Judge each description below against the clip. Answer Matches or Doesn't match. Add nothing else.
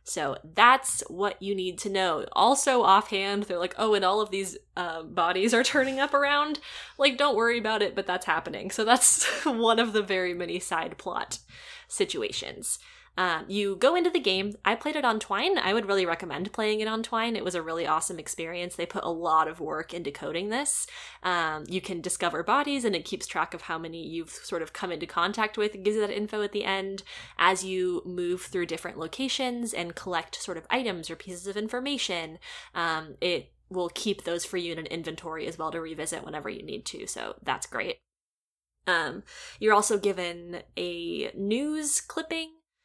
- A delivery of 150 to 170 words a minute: Doesn't match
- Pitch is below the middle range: Doesn't match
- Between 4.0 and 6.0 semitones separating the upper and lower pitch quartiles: Matches